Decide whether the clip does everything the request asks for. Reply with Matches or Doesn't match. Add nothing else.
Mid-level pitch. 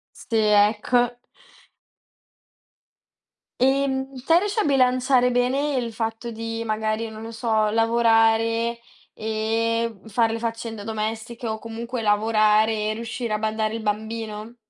Doesn't match